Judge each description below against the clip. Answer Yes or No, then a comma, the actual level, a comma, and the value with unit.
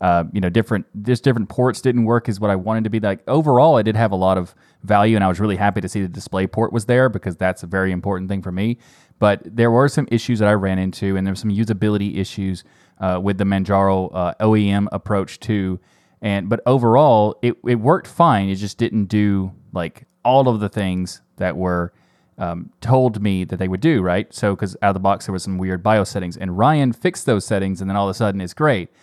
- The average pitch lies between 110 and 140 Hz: No, low, 100 Hz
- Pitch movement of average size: Yes, average, 3.4 semitones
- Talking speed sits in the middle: No, fast, 245 wpm